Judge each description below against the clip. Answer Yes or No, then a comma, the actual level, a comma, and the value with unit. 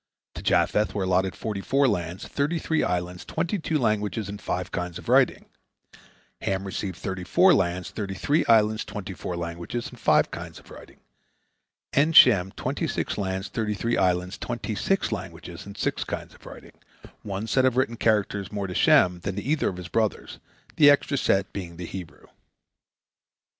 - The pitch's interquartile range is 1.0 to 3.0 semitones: No, average, 4.3 semitones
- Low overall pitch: Yes, low, 100 Hz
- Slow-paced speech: No, average, 175 wpm